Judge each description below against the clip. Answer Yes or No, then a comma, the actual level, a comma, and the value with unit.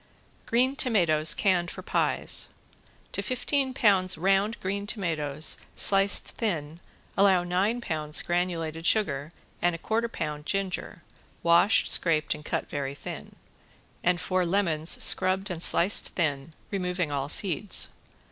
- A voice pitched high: No, medium, 180 Hz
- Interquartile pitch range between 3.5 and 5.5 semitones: Yes, average, 4.2 semitones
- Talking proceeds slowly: Yes, slow, 130 wpm